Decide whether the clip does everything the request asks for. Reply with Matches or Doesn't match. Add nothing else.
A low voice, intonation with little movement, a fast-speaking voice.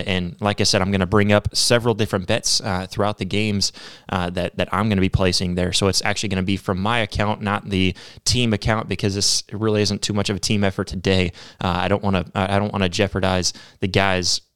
Matches